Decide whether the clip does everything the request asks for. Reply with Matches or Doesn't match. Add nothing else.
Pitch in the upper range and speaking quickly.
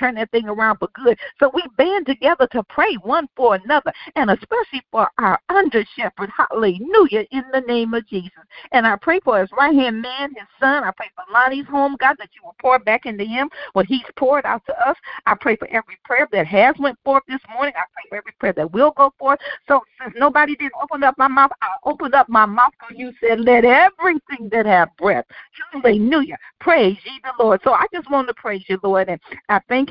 Matches